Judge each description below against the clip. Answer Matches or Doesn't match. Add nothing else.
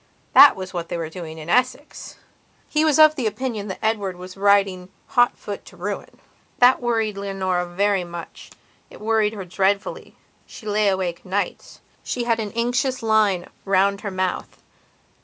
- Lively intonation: Doesn't match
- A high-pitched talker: Matches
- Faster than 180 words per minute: Doesn't match